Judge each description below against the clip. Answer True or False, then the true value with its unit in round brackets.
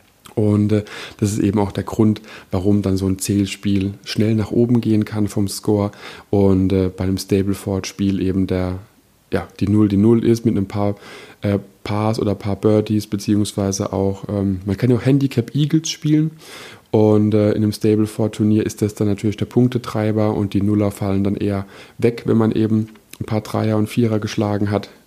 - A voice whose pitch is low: True (105 Hz)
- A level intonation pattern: True (1.6 semitones)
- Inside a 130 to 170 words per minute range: False (190 wpm)